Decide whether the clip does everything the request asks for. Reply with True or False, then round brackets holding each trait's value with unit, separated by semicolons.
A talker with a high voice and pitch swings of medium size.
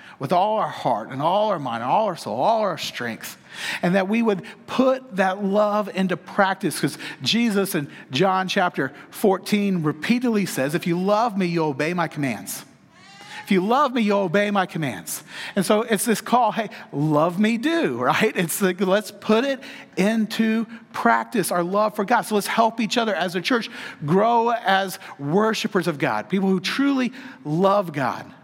True (200 Hz; 4.0 semitones)